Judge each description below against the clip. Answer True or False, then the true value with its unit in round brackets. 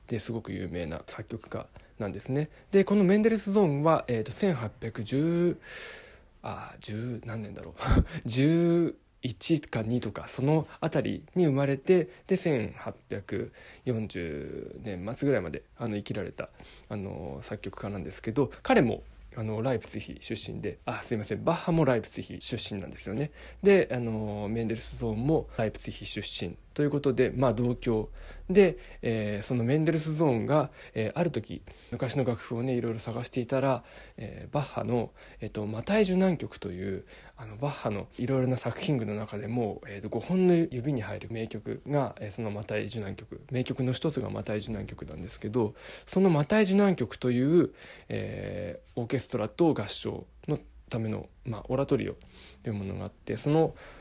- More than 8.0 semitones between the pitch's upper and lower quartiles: False (5.6 semitones)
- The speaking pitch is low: True (120 Hz)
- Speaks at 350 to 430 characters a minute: False (315 characters per minute)